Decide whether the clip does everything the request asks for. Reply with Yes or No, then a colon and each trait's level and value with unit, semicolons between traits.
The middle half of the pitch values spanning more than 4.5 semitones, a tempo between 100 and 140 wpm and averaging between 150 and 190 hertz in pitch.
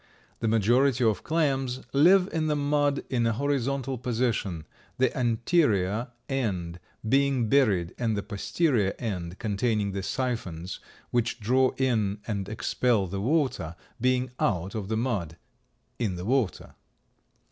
No: average, 4.9 semitones; slow, 135 wpm; low, 115 Hz